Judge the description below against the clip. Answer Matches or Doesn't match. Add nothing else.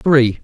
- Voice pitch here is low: Matches